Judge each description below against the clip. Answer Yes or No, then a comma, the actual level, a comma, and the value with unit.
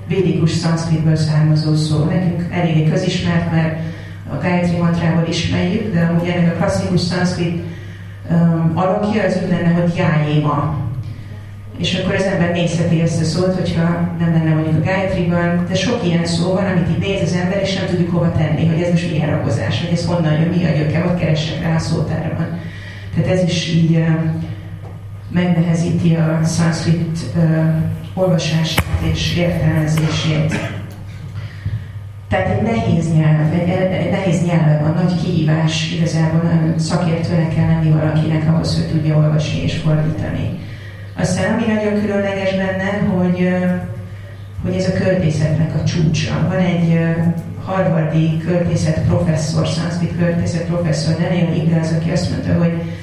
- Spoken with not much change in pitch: Yes, narrow, 2.1 semitones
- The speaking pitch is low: No, medium, 165 Hz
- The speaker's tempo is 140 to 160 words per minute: Yes, average, 150 wpm